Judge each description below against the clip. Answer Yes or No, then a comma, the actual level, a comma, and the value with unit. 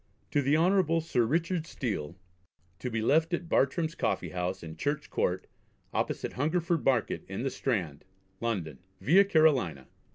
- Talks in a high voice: No, medium, 140 Hz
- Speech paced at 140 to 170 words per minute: Yes, average, 150 wpm